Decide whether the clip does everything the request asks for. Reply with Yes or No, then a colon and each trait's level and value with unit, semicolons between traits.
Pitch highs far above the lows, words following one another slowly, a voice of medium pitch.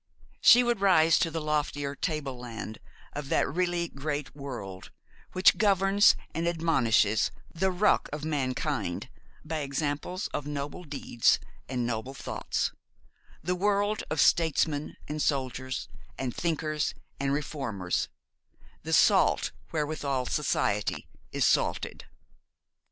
No: average, 3.9 semitones; slow, 120 wpm; medium, 150 Hz